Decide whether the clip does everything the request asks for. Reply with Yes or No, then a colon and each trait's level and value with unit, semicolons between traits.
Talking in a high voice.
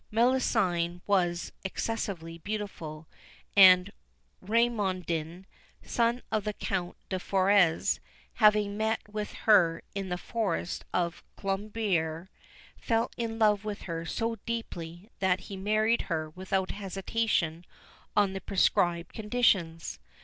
Yes: high, 195 Hz